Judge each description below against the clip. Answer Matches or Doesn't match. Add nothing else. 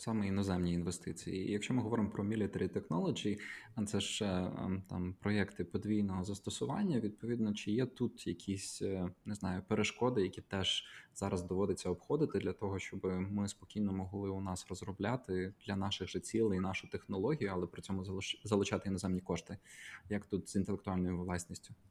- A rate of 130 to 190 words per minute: Matches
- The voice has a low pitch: Matches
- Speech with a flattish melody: Matches